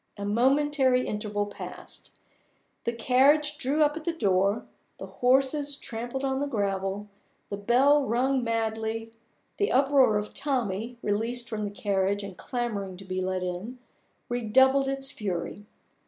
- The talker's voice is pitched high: Yes, high, 235 Hz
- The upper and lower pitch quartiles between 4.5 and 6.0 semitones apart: Yes, average, 4.8 semitones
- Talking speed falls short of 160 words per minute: Yes, average, 140 wpm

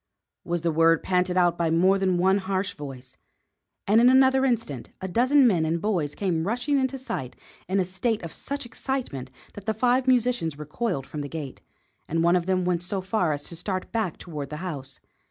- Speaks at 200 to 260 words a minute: Yes, fast, 205 wpm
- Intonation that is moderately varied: No, wide, 5.8 semitones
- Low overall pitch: No, medium, 185 Hz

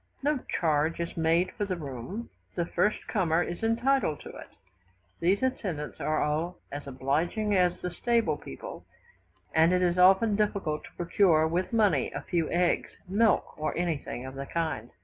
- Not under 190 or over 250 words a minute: No, average, 165 wpm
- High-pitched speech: No, medium, 175 Hz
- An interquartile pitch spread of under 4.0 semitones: No, average, 4.4 semitones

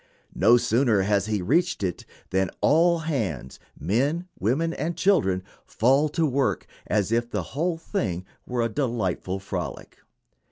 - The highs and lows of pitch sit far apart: Yes, wide, 8.4 semitones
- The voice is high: No, low, 120 Hz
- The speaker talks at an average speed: Yes, average, 145 wpm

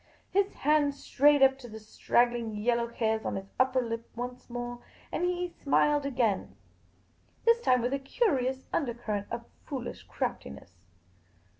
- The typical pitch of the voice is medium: No, very high, 250 Hz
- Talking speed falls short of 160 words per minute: Yes, average, 145 wpm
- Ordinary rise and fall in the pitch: Yes, average, 3.2 semitones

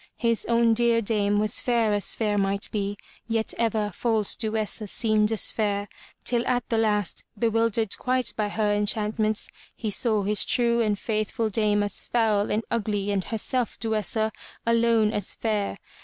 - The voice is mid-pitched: No, high, 215 Hz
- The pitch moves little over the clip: Yes, narrow, 1.8 semitones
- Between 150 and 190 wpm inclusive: Yes, average, 165 wpm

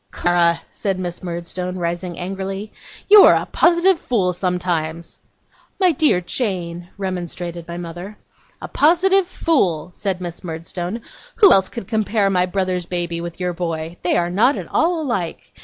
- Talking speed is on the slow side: No, average, 155 wpm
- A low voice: No, medium, 180 Hz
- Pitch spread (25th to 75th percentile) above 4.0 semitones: No, average, 3.7 semitones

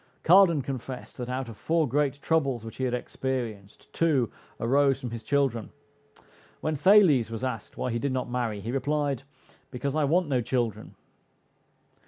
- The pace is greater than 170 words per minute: No, average, 165 wpm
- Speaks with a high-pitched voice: No, low, 130 Hz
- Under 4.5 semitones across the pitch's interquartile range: Yes, average, 3.4 semitones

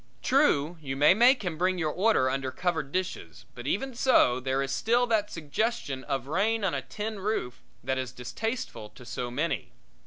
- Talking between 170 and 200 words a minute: Yes, average, 185 wpm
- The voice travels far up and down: Yes, wide, 8.5 semitones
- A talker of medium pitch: Yes, medium, 165 Hz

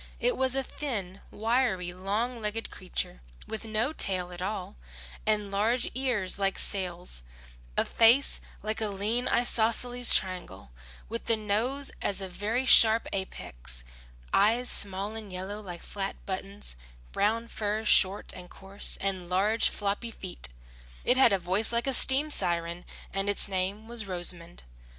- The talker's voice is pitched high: Yes, high, 205 Hz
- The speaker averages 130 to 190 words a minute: Yes, average, 150 wpm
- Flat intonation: No, average, 3.6 semitones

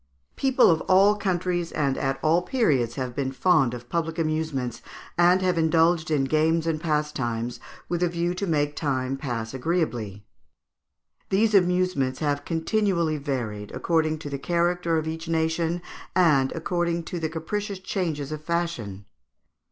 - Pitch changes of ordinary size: Yes, average, 4.1 semitones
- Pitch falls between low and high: Yes, medium, 160 Hz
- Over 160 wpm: No, average, 150 wpm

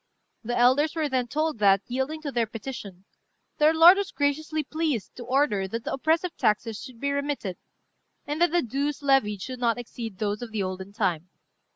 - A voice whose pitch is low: No, very high, 255 Hz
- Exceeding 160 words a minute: Yes, average, 190 wpm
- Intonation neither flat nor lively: No, wide, 5.8 semitones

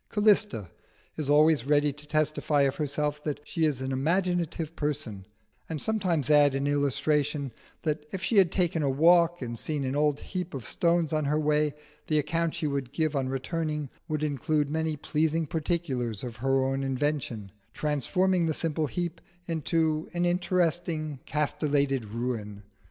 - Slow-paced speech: No, average, 160 wpm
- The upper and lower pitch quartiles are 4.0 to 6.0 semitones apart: No, average, 3.0 semitones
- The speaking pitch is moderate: Yes, medium, 150 Hz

